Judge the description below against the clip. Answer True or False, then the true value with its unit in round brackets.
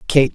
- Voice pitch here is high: False (140 Hz)